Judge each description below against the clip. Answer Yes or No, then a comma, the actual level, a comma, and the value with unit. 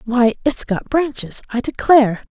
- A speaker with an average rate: Yes, average, 155 wpm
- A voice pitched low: No, very high, 250 Hz